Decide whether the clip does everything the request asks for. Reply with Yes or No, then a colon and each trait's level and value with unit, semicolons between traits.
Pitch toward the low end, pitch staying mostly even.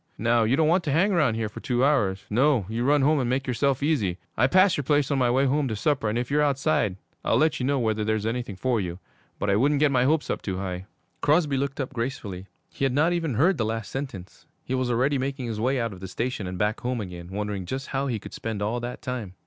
No: low, 125 Hz; average, 4.6 semitones